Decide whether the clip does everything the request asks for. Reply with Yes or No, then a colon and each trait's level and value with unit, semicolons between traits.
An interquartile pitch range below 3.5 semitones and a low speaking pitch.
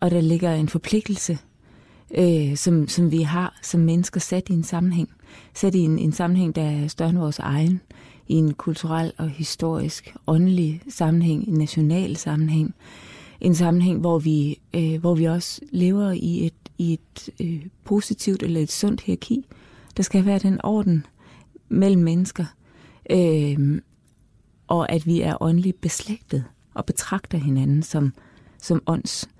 No: narrow, 2.4 semitones; medium, 170 Hz